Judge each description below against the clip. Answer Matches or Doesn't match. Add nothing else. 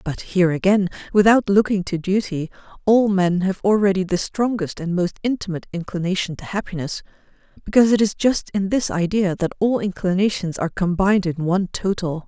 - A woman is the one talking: Matches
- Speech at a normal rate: Matches